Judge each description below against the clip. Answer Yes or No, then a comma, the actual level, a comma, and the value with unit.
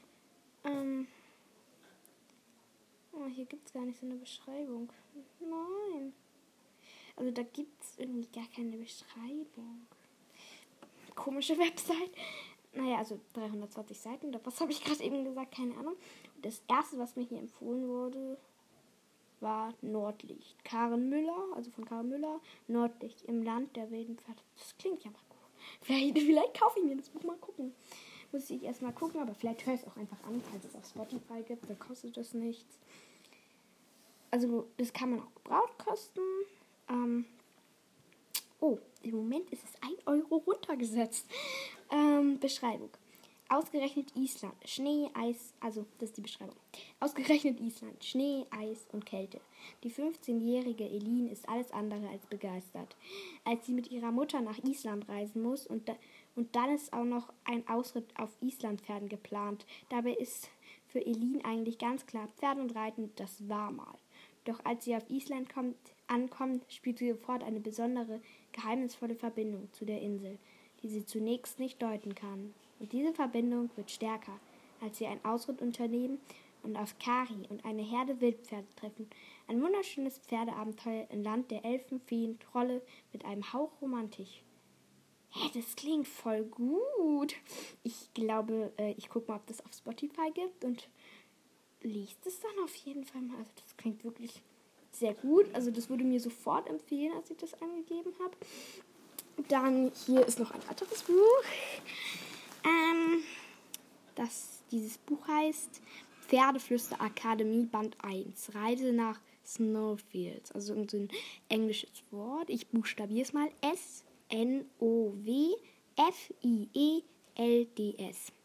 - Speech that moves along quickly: No, average, 145 wpm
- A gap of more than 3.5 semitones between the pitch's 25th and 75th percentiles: Yes, average, 3.9 semitones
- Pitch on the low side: No, high, 240 Hz